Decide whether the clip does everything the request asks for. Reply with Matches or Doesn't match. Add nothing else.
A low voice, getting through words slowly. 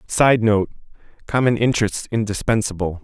Matches